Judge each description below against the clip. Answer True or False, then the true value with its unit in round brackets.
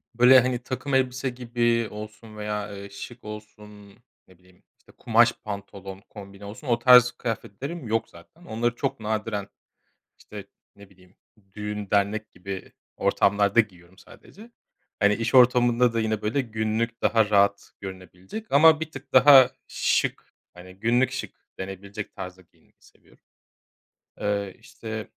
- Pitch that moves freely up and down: False (3.4 semitones)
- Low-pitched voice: True (110 Hz)